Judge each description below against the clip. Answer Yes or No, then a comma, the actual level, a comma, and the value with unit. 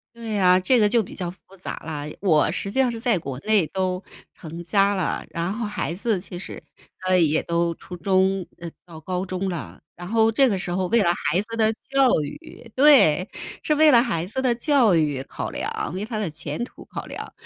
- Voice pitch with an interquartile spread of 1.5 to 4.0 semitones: No, average, 4.9 semitones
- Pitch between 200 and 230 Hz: No, high, 190 Hz